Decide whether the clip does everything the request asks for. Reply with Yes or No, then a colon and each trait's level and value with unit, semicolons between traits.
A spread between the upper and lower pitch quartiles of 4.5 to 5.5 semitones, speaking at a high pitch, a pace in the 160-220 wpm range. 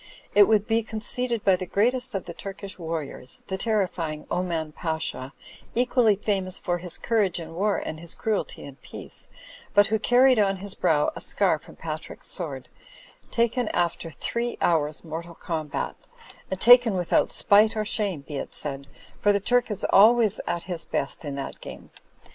Yes: average, 4.9 semitones; high, 195 Hz; average, 180 wpm